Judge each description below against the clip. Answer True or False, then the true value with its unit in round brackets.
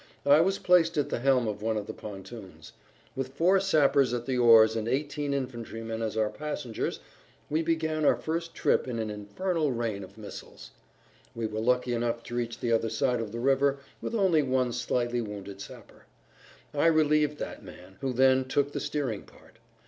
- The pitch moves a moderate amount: True (4.7 semitones)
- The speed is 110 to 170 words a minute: False (185 wpm)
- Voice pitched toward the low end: True (125 Hz)